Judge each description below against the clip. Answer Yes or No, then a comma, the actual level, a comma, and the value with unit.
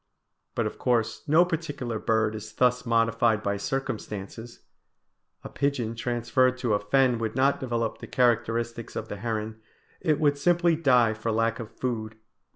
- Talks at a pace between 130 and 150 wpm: No, average, 160 wpm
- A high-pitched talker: No, low, 115 Hz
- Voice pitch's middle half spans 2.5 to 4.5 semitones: Yes, average, 2.8 semitones